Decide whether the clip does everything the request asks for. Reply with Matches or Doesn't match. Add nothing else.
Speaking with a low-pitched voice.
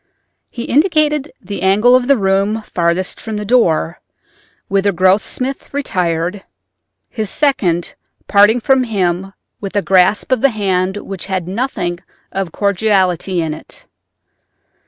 Doesn't match